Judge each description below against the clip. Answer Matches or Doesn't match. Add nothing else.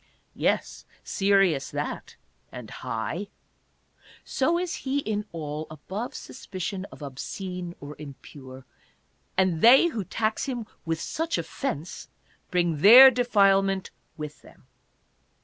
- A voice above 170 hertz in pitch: Matches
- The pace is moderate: Doesn't match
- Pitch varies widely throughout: Matches